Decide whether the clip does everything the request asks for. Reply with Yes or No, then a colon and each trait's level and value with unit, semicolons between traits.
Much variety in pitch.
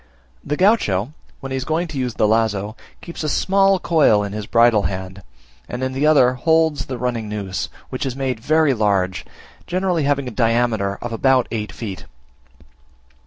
Yes: wide, 5.7 semitones